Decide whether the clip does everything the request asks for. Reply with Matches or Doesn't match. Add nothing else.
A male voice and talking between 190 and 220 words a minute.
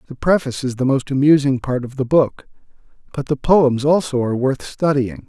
Matches